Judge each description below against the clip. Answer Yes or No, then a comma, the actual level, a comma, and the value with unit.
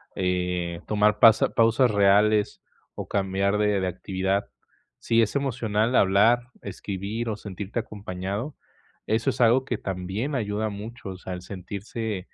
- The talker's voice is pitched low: Yes, low, 105 Hz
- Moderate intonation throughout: Yes, average, 3.0 semitones